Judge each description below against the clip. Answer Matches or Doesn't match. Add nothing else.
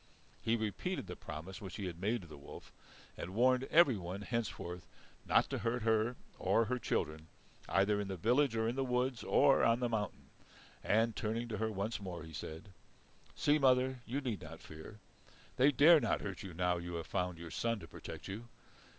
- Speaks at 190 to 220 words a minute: Matches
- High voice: Doesn't match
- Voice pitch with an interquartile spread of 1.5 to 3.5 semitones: Doesn't match